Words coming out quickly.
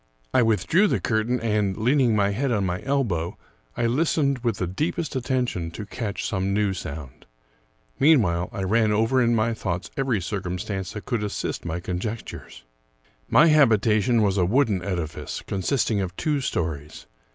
No: average, 160 wpm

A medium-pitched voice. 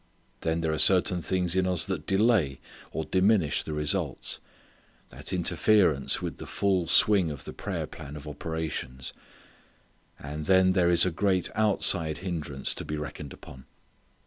No: very low, 85 Hz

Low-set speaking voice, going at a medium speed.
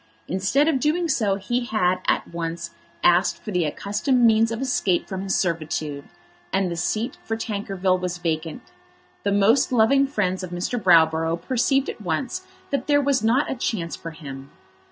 No: high, 195 Hz; average, 175 wpm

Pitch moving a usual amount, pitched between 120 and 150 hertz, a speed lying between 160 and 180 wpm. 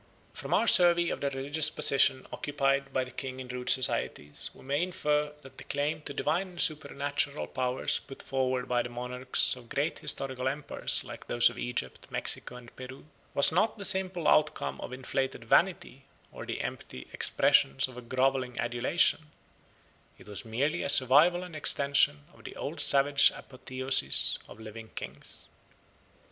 Yes: average, 3.0 semitones; low, 135 Hz; average, 165 wpm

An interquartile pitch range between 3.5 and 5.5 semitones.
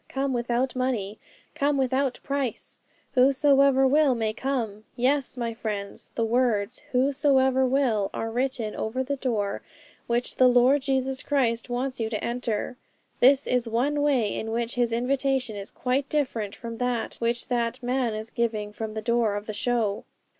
No: average, 2.8 semitones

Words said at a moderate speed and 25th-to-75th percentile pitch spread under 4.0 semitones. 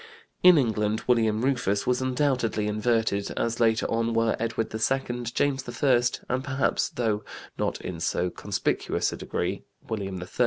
Yes: average, 150 wpm; average, 2.9 semitones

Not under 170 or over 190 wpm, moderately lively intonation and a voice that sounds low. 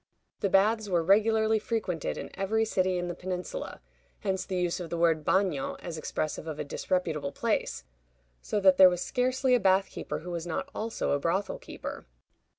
No: average, 185 wpm; average, 4.0 semitones; medium, 185 Hz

